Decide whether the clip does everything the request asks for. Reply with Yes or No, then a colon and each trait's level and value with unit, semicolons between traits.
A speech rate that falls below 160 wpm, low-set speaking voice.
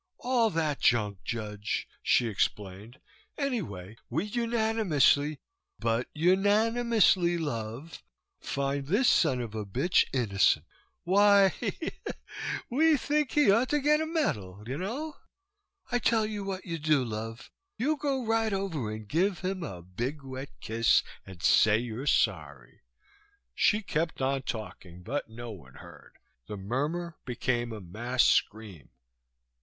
No: average, 140 wpm; medium, 145 Hz